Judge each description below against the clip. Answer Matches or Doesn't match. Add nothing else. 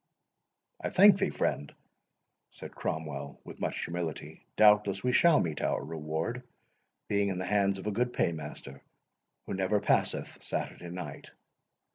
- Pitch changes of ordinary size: Matches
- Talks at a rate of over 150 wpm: Doesn't match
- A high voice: Doesn't match